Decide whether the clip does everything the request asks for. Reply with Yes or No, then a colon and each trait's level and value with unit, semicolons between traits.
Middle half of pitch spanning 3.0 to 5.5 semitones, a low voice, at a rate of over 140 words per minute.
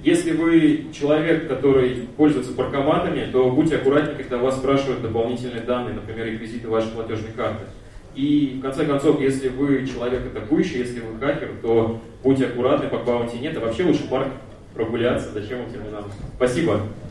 Yes: average, 3.7 semitones; low, 130 Hz; fast, 160 wpm